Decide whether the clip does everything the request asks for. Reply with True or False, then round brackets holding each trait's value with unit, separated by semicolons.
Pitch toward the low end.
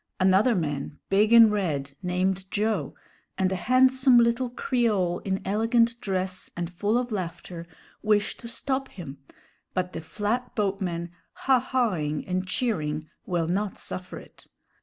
False (195 Hz)